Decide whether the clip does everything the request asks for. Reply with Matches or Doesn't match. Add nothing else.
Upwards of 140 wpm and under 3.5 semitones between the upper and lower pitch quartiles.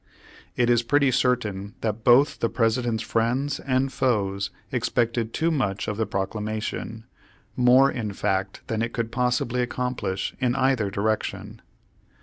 Doesn't match